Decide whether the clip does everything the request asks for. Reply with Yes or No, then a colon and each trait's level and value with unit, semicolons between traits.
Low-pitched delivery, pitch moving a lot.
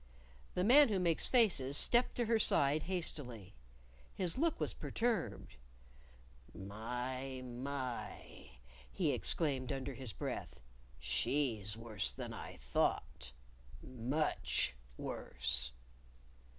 Yes: low, 130 Hz; wide, 7.4 semitones